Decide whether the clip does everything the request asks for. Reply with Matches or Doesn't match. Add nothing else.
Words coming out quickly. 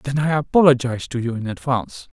Doesn't match